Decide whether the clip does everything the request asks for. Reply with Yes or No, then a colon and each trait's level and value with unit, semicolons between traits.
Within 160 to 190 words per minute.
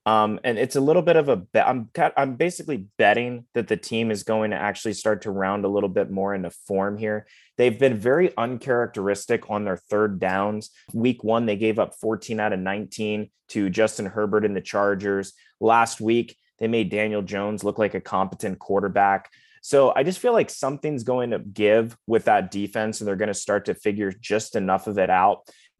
No: fast, 205 wpm